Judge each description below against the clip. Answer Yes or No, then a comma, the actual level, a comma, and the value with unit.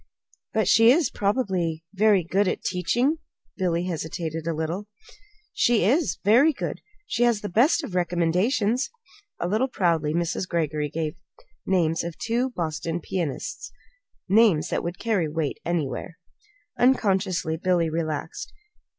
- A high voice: No, medium, 180 Hz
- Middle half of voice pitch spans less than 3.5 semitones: No, average, 5.0 semitones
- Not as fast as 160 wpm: Yes, slow, 135 wpm